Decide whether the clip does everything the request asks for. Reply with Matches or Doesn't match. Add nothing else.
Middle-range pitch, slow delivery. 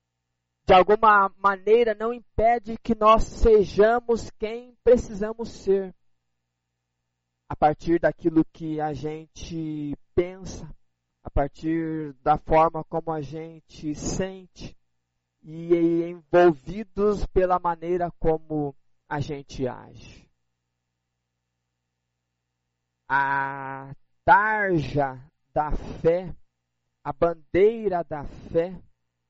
Matches